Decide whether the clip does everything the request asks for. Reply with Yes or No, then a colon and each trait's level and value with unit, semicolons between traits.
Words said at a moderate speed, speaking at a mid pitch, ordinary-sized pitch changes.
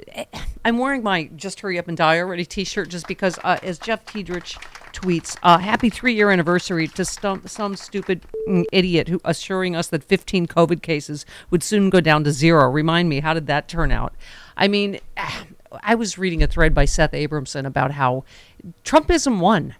Yes: average, 185 wpm; medium, 175 Hz; average, 3.7 semitones